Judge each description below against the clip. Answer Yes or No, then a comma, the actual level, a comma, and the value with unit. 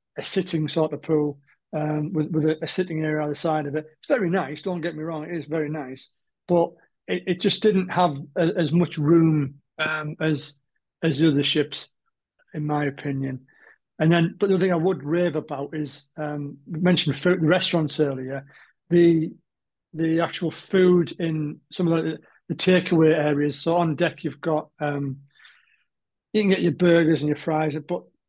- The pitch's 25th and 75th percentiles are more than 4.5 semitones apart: No, narrow, 2.4 semitones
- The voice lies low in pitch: No, medium, 160 Hz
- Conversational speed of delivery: Yes, average, 195 wpm